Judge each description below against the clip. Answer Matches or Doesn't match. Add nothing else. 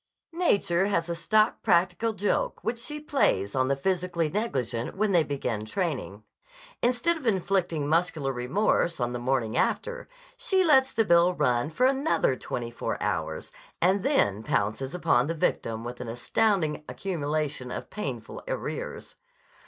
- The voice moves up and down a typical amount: Doesn't match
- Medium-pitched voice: Matches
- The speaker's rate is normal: Matches